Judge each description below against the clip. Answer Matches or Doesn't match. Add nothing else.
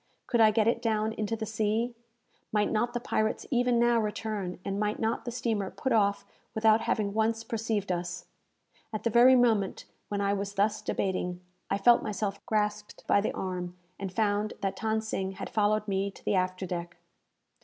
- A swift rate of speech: Doesn't match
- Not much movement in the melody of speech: Matches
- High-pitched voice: Matches